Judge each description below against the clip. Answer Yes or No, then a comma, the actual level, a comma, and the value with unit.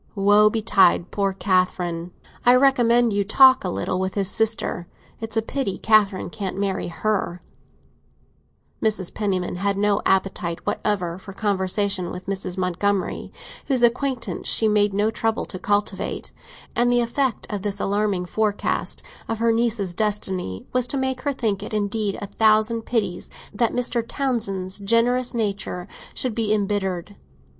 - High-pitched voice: Yes, high, 205 Hz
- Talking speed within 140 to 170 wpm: Yes, average, 150 wpm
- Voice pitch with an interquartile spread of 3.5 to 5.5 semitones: No, average, 3.1 semitones